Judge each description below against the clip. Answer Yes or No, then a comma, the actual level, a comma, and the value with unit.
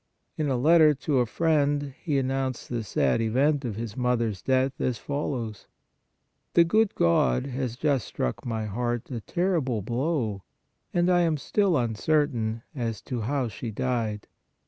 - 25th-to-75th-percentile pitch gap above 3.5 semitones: Yes, average, 4.5 semitones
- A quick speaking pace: No, average, 165 wpm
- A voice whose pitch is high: No, low, 125 Hz